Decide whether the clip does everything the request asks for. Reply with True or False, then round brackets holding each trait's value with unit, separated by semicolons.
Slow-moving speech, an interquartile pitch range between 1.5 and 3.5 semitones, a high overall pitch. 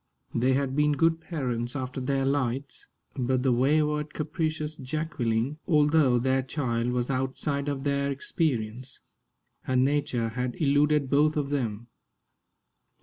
False (130 wpm; 2.9 semitones; 140 Hz)